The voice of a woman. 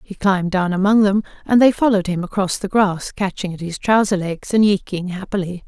Yes: female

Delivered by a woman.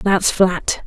Yes: female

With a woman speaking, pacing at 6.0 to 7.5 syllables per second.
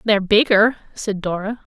No: female; 4.9 syllables/s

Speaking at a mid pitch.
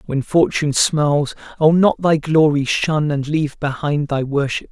Yes: medium, 150 Hz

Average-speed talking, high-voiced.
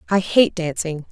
No: average, 160 wpm; medium, 175 Hz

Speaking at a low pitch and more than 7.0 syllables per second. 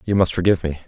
Yes: very low, 90 Hz; 8.5 syllables/s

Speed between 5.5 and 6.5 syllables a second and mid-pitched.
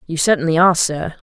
Yes: 6.4 syllables/s; medium, 165 Hz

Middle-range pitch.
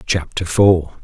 No: very low, 85 Hz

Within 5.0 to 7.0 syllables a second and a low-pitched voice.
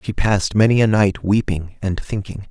Yes: 5.2 syllables/s; low, 100 Hz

